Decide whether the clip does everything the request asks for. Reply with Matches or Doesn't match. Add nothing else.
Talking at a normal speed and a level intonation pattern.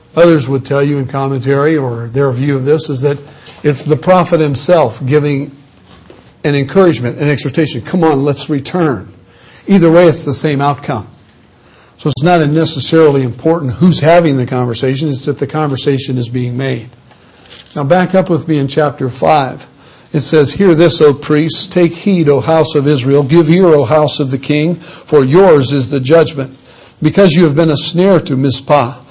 Doesn't match